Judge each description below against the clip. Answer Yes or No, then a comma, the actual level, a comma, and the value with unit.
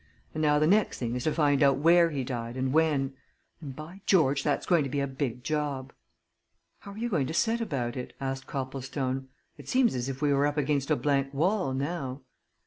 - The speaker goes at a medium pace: No, fast, 220 wpm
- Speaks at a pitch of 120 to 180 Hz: Yes, medium, 140 Hz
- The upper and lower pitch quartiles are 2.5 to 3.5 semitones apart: Yes, average, 2.9 semitones